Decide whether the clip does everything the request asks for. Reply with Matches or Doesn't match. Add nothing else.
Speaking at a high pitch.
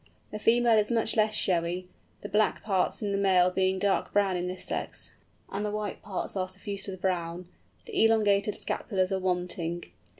Matches